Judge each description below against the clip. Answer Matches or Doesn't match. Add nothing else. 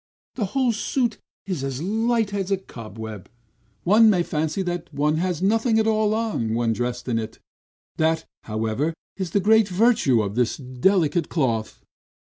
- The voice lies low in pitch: Doesn't match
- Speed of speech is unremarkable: Matches